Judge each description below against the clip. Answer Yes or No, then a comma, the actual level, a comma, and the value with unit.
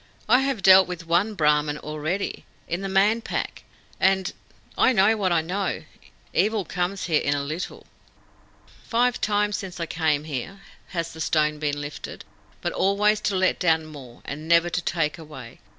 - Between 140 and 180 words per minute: Yes, average, 170 wpm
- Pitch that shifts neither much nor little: Yes, average, 4.4 semitones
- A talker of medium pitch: Yes, medium, 175 Hz